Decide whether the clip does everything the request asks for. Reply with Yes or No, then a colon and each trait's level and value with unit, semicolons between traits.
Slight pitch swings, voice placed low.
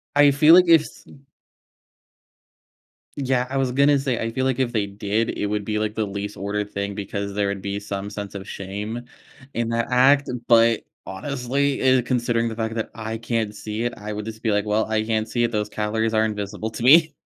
No: average, 3.1 semitones; low, 110 Hz